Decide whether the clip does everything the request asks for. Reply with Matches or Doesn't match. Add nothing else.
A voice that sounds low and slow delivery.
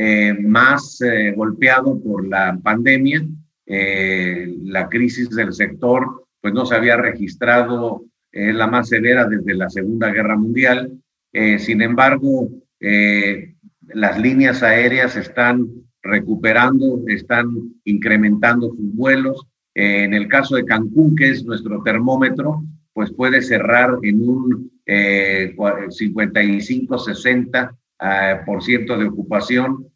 Matches